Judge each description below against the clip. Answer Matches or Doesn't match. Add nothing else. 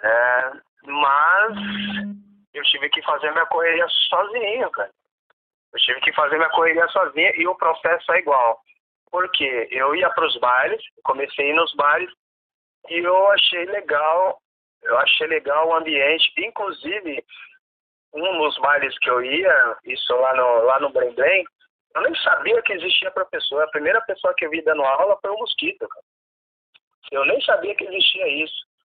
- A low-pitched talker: Doesn't match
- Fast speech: Doesn't match